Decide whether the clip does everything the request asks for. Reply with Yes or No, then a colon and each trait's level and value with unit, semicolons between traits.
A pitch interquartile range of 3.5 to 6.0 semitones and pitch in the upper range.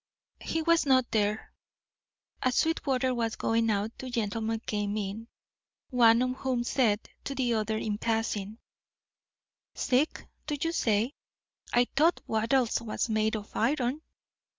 No: average, 3.0 semitones; high, 230 Hz